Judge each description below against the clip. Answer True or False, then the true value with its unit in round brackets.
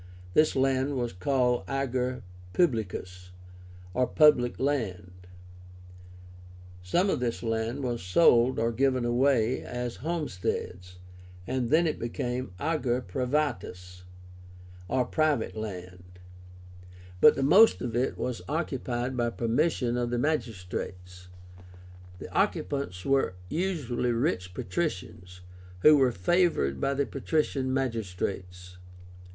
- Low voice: True (125 Hz)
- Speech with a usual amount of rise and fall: False (6.2 semitones)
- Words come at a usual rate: False (110 wpm)